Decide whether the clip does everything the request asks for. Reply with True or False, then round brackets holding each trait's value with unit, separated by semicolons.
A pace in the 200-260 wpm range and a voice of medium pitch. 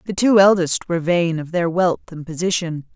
True (205 wpm; 175 Hz)